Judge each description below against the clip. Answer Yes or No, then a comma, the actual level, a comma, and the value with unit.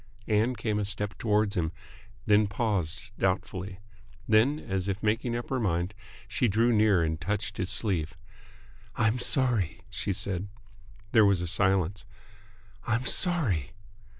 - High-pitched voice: No, low, 105 Hz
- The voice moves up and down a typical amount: Yes, average, 3.0 semitones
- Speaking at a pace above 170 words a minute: No, average, 140 wpm